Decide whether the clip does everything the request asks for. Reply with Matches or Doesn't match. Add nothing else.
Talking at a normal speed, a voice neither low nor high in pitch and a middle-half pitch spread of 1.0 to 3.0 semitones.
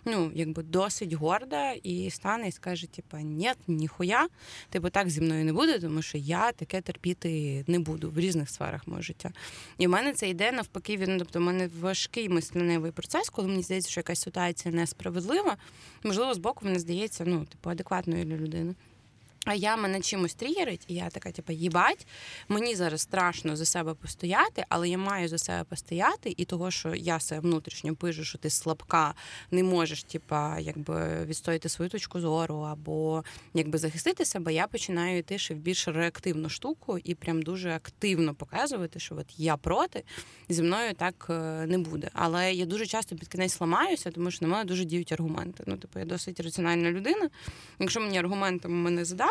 Doesn't match